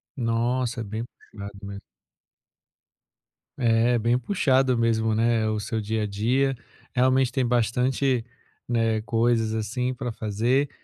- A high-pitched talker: No, low, 115 Hz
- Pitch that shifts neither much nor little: No, narrow, 2.2 semitones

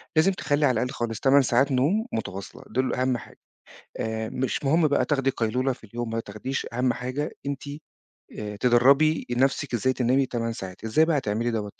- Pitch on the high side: No, low, 125 Hz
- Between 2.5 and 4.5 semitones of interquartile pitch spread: Yes, average, 3.4 semitones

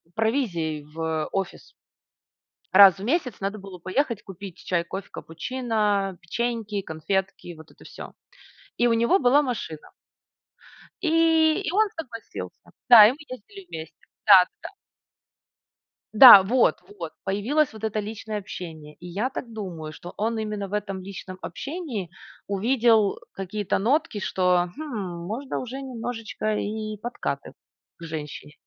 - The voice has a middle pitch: No, high, 210 Hz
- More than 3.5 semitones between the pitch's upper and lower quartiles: Yes, average, 5.0 semitones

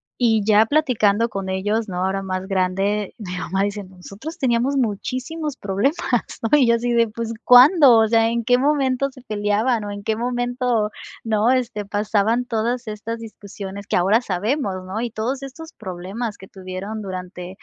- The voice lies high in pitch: Yes, high, 220 Hz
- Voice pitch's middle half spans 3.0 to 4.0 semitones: Yes, average, 3.7 semitones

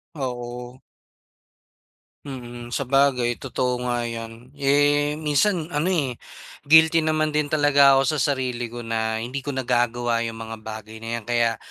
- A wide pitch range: No, average, 3.4 semitones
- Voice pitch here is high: No, low, 125 Hz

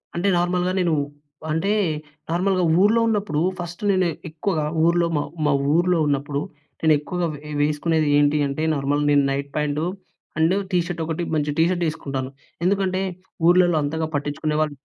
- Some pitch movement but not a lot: Yes, average, 3.2 semitones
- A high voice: No, medium, 160 Hz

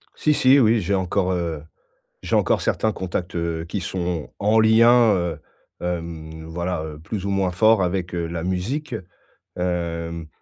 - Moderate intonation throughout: Yes, average, 3.6 semitones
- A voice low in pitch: Yes, very low, 90 Hz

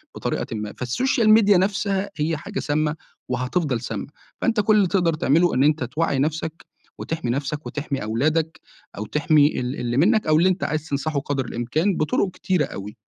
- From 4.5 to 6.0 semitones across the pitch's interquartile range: Yes, average, 5.0 semitones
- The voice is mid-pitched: Yes, medium, 155 Hz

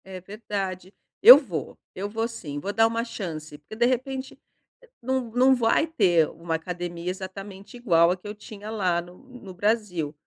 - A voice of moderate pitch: No, high, 200 Hz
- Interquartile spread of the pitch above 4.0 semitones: Yes, average, 4.6 semitones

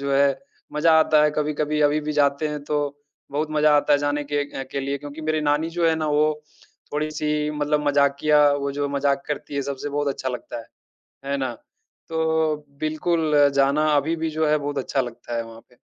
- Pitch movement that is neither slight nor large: No, narrow, 1.4 semitones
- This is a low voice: No, medium, 145 Hz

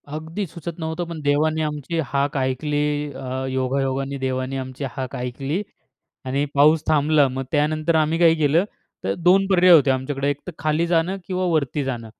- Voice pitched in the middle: Yes, medium, 145 Hz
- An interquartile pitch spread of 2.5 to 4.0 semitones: Yes, average, 3.2 semitones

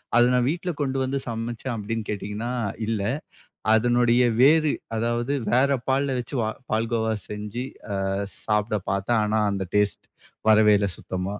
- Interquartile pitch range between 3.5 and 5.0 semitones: No, average, 2.8 semitones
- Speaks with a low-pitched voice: Yes, low, 115 Hz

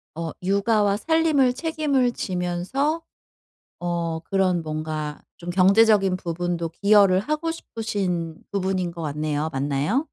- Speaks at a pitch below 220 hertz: Yes, medium, 185 Hz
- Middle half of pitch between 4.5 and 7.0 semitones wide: Yes, average, 5.2 semitones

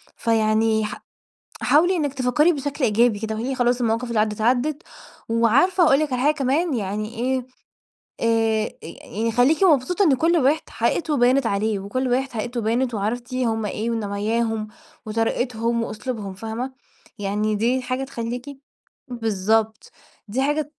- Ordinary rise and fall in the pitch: Yes, average, 3.3 semitones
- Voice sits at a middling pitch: No, high, 235 Hz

